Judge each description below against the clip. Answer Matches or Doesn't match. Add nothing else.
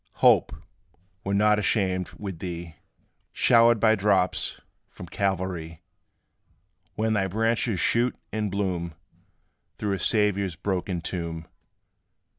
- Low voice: Matches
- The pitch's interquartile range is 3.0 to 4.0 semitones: Matches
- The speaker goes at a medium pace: Doesn't match